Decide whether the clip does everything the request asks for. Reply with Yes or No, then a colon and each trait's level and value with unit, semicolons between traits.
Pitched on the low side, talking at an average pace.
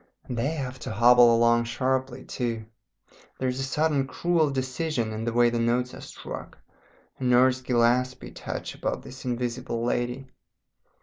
Yes: low, 125 Hz; average, 160 wpm